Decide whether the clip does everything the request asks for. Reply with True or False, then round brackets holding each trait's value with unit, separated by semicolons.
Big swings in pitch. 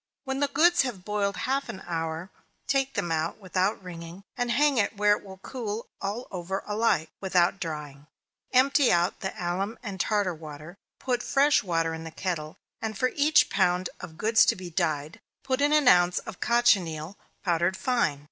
True (6.0 semitones)